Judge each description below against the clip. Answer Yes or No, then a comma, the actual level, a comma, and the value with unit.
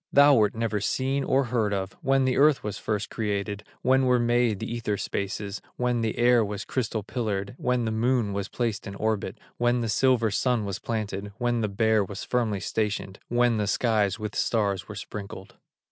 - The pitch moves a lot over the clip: No, average, 3.1 semitones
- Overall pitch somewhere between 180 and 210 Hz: No, low, 110 Hz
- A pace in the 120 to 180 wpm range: No, average, 190 wpm